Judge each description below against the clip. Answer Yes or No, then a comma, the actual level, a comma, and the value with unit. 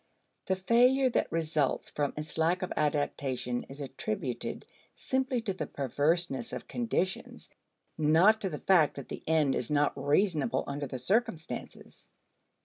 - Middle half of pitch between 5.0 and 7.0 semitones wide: Yes, average, 5.3 semitones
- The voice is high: No, medium, 160 Hz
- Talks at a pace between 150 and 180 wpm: No, average, 140 wpm